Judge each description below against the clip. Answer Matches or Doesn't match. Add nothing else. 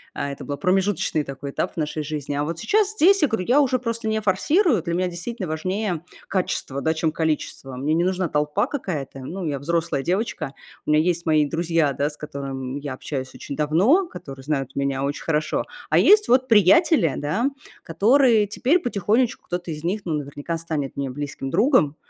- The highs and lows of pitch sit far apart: Matches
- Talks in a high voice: Doesn't match